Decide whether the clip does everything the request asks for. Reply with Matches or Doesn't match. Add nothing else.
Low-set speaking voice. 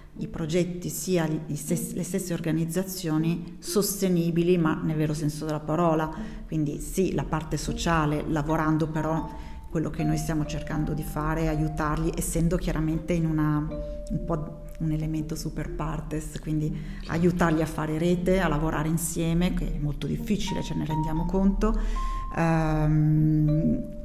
Doesn't match